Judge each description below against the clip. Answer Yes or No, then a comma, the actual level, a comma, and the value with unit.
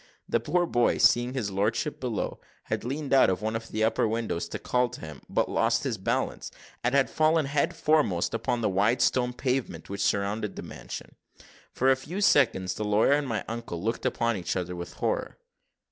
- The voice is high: No, low, 115 Hz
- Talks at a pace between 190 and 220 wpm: Yes, average, 200 wpm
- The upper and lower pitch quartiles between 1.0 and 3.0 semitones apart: No, average, 4.6 semitones